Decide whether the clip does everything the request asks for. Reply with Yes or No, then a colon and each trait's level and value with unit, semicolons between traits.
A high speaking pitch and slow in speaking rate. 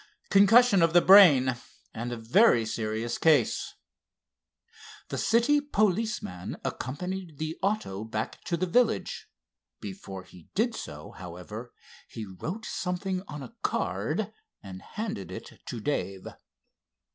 No: medium, 155 Hz; slow, 120 wpm